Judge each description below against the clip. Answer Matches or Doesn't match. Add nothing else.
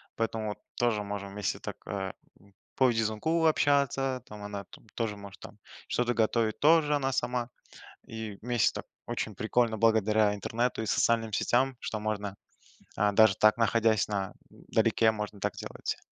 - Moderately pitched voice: Doesn't match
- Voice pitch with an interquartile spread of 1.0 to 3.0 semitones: Matches